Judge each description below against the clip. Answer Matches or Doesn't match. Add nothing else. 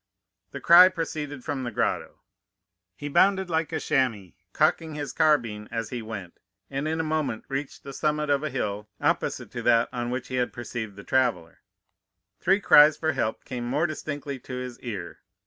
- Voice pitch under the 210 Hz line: Matches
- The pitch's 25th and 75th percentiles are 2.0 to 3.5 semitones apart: Doesn't match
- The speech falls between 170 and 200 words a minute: Matches